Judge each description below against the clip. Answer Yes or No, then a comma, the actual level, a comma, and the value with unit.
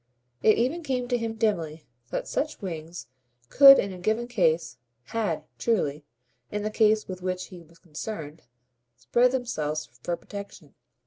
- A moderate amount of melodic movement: No, wide, 5.9 semitones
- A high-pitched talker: Yes, high, 200 Hz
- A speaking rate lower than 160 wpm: Yes, average, 150 wpm